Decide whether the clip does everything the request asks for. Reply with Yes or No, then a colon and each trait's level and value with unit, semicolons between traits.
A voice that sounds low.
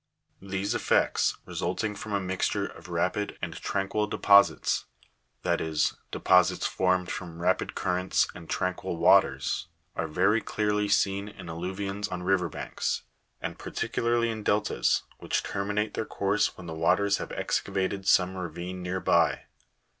Yes: very low, 95 Hz